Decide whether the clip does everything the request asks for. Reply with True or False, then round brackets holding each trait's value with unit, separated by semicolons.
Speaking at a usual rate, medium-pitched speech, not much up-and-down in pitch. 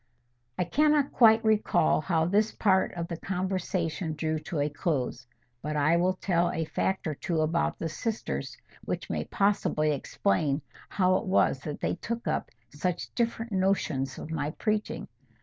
False (165 wpm; 175 Hz; 4.4 semitones)